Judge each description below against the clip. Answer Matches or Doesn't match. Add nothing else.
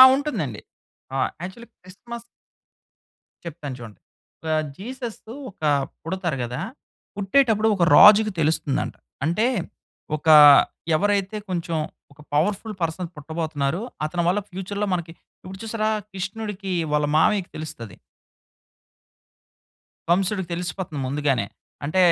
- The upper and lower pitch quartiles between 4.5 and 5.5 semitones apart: Matches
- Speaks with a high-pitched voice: Doesn't match